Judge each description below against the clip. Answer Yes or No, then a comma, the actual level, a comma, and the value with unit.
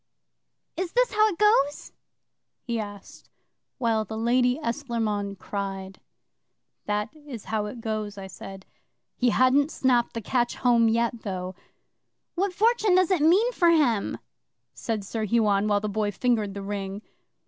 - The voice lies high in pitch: Yes, high, 230 Hz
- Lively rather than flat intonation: Yes, wide, 5.8 semitones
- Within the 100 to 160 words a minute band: Yes, average, 150 wpm